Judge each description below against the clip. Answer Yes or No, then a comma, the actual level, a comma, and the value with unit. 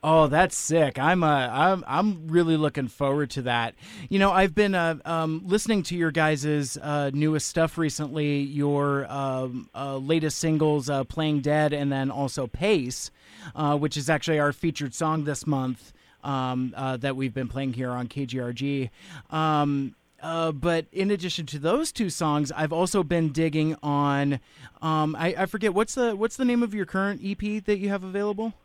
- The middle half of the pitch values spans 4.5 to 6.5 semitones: No, average, 3.8 semitones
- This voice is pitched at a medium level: Yes, medium, 155 Hz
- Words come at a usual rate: Yes, average, 180 wpm